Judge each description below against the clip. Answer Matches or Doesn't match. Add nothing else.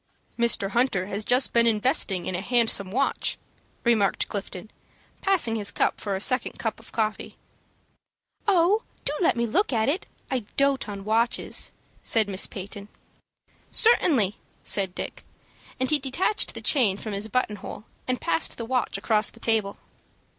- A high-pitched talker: Matches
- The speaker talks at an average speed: Matches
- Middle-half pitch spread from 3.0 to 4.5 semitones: Matches